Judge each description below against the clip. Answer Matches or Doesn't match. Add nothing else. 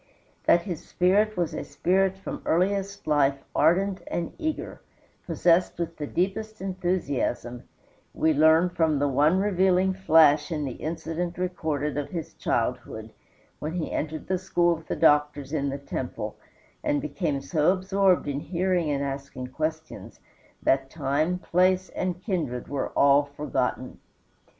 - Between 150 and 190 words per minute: Doesn't match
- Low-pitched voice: Doesn't match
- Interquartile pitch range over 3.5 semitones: Matches